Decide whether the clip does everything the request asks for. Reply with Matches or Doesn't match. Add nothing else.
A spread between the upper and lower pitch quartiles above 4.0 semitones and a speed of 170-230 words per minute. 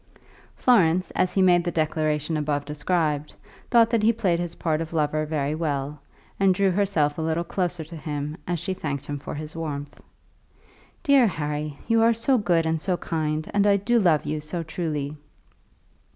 Doesn't match